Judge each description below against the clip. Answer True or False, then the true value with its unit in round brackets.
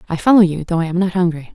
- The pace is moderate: False (310 wpm)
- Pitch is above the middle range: False (175 Hz)